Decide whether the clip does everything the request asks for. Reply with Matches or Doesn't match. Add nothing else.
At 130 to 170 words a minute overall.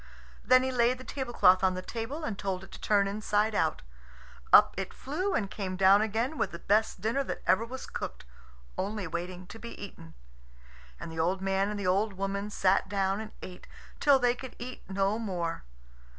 Doesn't match